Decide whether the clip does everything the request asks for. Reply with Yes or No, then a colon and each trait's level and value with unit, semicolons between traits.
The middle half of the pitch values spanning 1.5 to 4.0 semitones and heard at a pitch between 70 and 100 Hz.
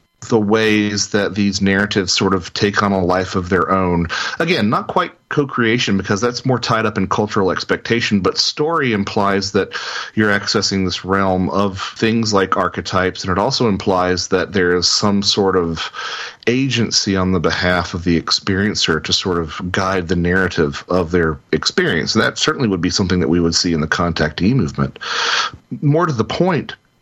Yes: average, 2.9 semitones; very low, 95 Hz